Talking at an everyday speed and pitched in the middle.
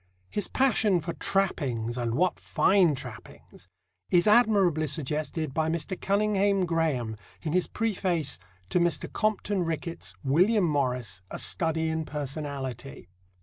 No: slow, 125 wpm; medium, 160 Hz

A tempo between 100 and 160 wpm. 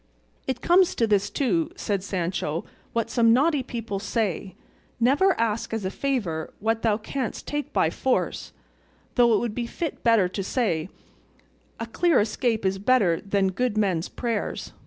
Yes: average, 155 wpm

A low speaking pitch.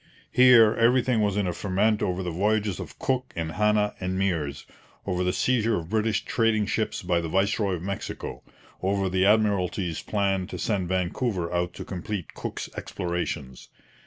Yes: very low, 95 Hz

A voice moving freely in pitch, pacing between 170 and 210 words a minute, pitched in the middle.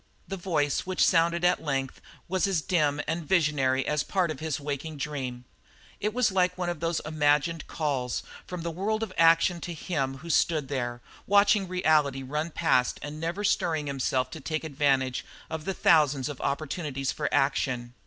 No: average, 3.9 semitones; average, 175 wpm; medium, 155 Hz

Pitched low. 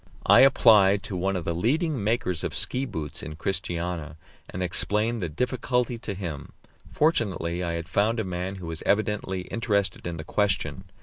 Yes: very low, 95 Hz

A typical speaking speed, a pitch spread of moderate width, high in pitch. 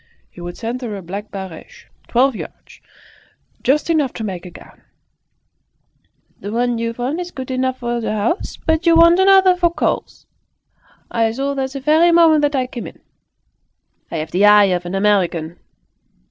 No: average, 175 wpm; wide, 6.8 semitones; high, 245 Hz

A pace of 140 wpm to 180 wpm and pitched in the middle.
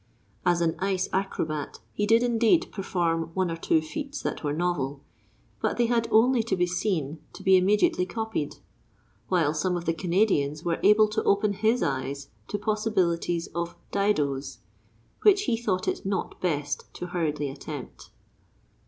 Yes: average, 160 wpm; medium, 180 Hz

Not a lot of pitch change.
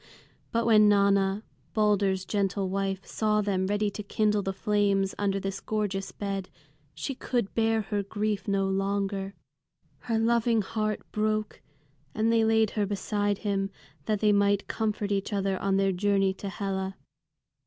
Yes: narrow, 1.6 semitones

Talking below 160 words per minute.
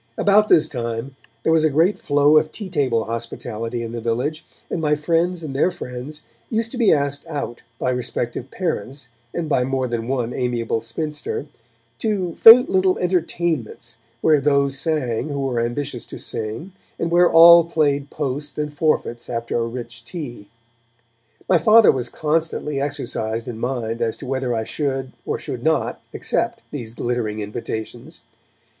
No: average, 165 wpm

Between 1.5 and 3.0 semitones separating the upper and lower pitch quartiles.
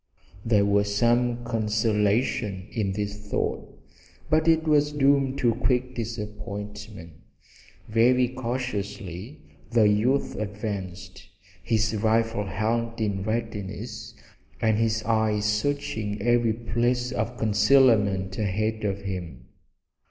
Yes: average, 2.7 semitones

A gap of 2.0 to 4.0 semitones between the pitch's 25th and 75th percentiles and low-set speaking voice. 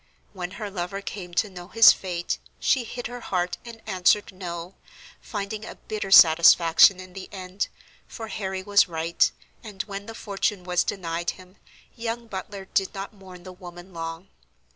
No: narrow, 2.5 semitones; high, 190 Hz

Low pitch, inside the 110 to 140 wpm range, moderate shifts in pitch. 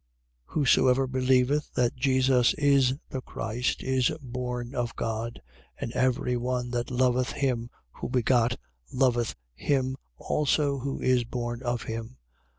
No: low, 125 Hz; slow, 135 wpm; narrow, 1.6 semitones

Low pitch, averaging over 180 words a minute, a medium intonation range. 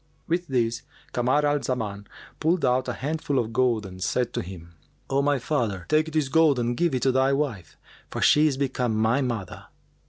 Yes: low, 130 Hz; average, 195 wpm; average, 4.2 semitones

